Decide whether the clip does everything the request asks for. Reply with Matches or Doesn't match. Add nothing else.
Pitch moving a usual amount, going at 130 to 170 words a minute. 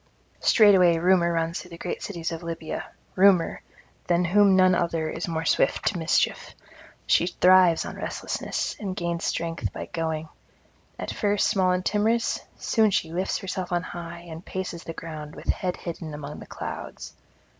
Doesn't match